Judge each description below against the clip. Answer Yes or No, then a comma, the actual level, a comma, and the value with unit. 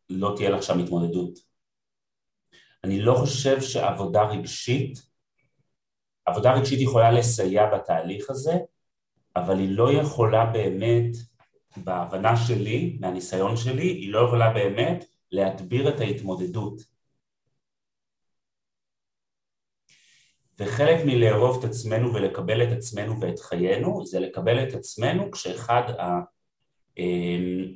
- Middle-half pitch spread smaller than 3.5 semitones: No, average, 5.0 semitones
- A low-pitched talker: Yes, low, 115 Hz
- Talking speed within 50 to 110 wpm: Yes, slow, 100 wpm